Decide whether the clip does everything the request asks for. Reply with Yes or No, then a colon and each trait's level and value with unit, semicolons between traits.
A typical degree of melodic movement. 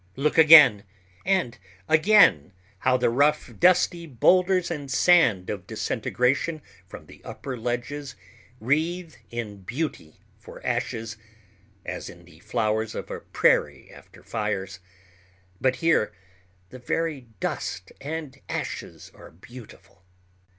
No: wide, 7.7 semitones